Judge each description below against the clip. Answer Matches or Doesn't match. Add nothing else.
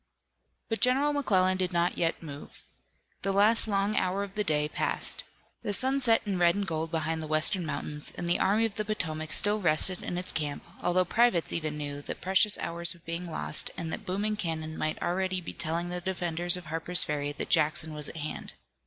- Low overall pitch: Doesn't match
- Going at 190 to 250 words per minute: Matches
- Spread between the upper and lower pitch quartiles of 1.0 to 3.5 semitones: Doesn't match